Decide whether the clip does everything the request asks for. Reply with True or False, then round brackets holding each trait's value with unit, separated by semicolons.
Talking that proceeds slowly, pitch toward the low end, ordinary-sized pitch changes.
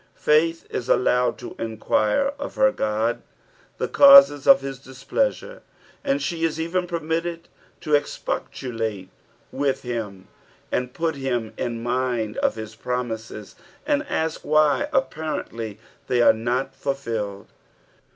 False (130 wpm; 130 Hz; 6.4 semitones)